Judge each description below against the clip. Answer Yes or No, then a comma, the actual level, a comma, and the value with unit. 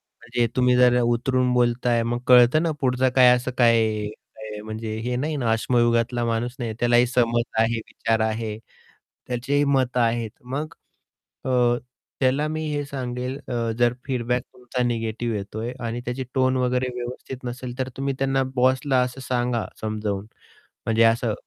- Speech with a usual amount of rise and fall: No, narrow, 1.7 semitones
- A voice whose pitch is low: Yes, low, 120 Hz